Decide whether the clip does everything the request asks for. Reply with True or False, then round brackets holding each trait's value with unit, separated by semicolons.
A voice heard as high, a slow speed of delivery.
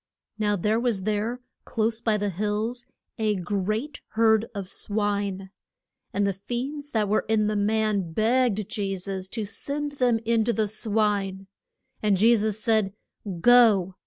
False (215 Hz; 155 wpm)